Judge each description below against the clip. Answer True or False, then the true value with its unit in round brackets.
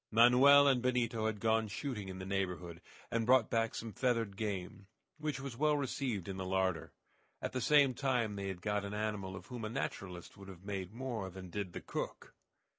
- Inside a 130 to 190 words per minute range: False (200 wpm)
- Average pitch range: True (4.4 semitones)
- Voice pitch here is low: True (110 Hz)